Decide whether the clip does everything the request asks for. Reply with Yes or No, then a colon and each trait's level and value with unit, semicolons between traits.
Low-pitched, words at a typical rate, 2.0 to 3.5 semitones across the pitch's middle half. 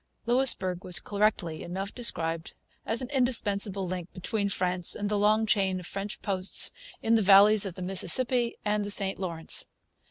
No: high, 200 Hz; average, 165 wpm; average, 2.8 semitones